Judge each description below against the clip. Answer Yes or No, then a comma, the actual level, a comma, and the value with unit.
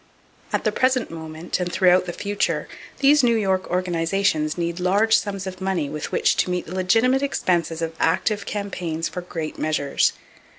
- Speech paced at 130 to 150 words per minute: No, average, 170 wpm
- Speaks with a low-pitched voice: No, medium, 180 Hz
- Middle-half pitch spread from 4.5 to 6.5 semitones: No, average, 3.5 semitones